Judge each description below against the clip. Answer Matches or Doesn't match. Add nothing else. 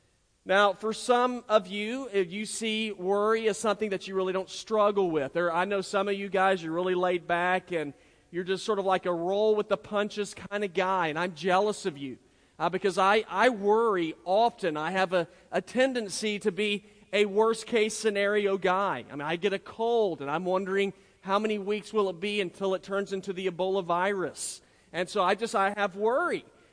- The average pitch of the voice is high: Matches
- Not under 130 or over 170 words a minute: Doesn't match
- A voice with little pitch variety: Matches